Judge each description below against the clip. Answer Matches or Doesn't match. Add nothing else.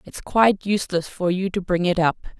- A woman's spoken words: Matches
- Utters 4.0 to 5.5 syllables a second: Doesn't match